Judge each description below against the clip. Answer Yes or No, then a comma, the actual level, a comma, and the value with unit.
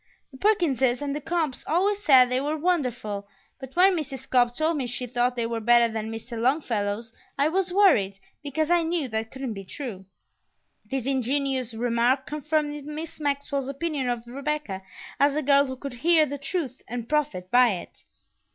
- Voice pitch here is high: Yes, very high, 270 Hz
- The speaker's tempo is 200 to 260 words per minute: No, average, 180 wpm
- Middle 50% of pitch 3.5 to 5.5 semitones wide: Yes, average, 4.1 semitones